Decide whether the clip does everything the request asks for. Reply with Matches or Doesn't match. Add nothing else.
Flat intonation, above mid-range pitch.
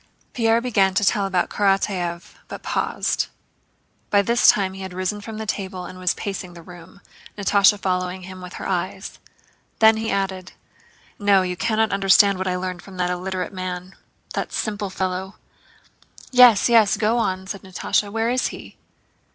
Matches